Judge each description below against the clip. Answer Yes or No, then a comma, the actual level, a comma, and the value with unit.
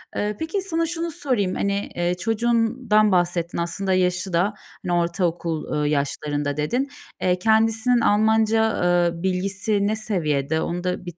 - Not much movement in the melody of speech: No, average, 4.3 semitones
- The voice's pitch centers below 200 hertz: Yes, high, 190 Hz